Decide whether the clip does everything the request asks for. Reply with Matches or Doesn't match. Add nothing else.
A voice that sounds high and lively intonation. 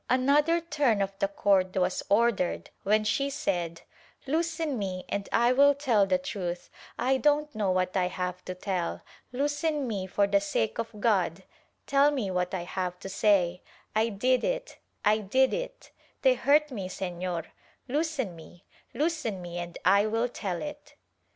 Matches